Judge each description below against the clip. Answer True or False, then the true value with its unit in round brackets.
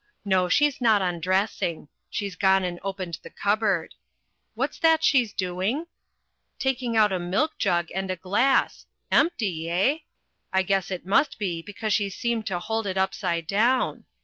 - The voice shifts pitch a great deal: False (3.8 semitones)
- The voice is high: True (195 Hz)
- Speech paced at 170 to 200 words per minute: False (155 wpm)